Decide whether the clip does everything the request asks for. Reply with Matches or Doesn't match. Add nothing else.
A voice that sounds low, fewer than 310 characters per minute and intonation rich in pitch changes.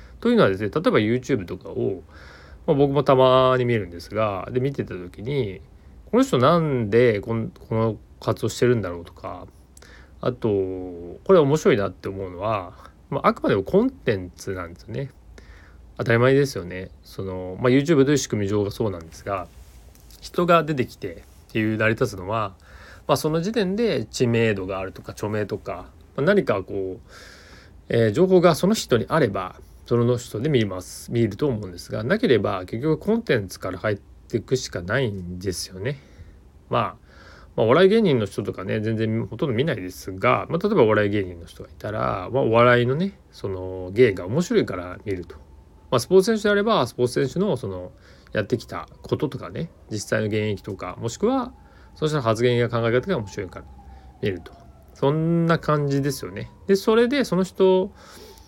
Doesn't match